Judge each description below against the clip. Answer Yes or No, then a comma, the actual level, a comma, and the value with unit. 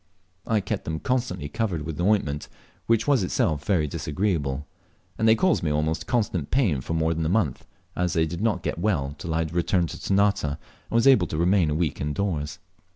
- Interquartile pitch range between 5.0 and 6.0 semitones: Yes, average, 5.3 semitones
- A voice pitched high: No, very low, 85 Hz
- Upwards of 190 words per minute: Yes, fast, 205 wpm